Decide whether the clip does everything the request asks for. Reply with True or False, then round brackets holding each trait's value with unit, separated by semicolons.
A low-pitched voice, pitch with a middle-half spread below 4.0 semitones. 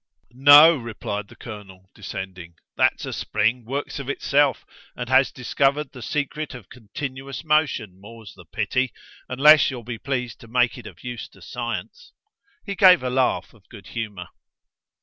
False (125 Hz; 4.5 semitones)